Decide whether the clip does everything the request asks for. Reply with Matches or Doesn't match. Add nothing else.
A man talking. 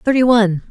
Doesn't match